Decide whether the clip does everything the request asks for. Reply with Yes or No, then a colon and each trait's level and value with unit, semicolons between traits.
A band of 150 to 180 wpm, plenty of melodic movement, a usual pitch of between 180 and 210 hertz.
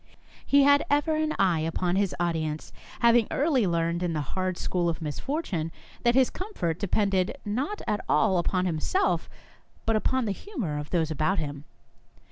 Yes: average, 170 wpm; wide, 7.8 semitones; medium, 185 Hz